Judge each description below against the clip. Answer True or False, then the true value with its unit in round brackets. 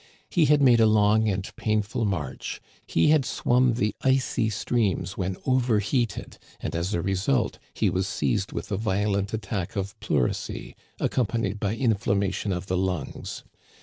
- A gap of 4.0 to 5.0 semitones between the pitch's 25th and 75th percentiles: False (3.4 semitones)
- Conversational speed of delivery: True (160 wpm)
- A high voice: False (105 Hz)